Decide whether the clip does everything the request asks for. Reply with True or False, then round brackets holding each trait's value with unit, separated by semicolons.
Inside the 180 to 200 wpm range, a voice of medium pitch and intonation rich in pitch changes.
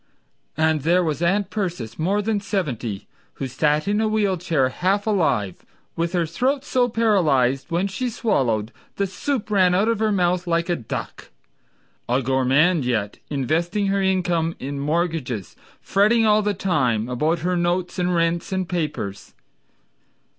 False (155 wpm; 175 Hz; 6.0 semitones)